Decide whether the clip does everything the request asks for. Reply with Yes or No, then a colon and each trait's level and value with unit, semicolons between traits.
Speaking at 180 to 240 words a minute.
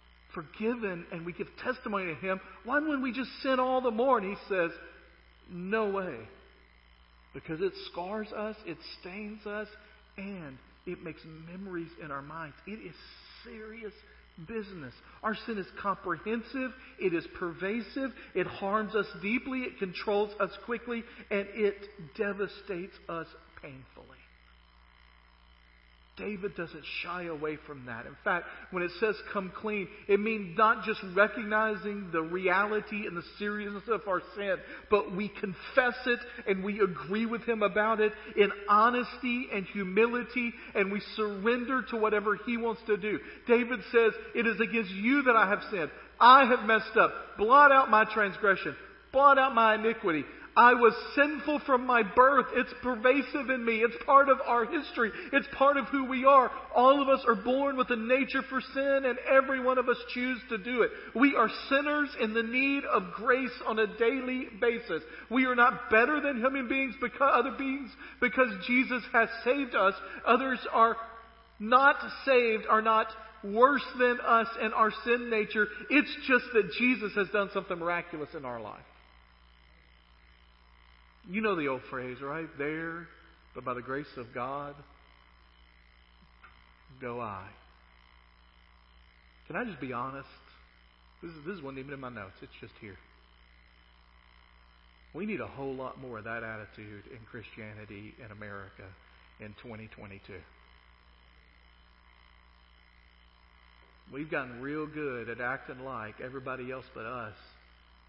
No: average, 155 wpm